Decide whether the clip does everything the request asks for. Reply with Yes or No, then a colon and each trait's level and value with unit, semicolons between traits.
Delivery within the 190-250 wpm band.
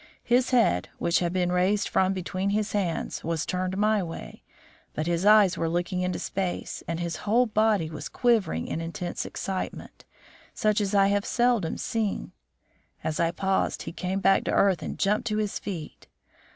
No: average, 180 wpm